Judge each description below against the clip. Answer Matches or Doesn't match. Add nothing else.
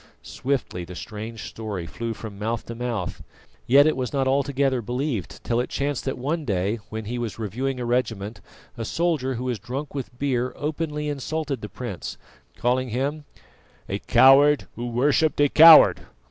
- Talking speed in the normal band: Matches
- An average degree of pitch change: Matches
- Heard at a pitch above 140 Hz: Doesn't match